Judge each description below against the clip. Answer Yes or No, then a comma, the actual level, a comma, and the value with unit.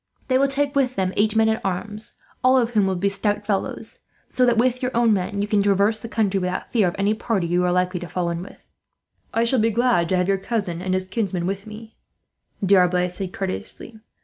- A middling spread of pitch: Yes, average, 3.5 semitones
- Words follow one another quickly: Yes, fast, 230 wpm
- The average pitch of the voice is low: No, high, 205 Hz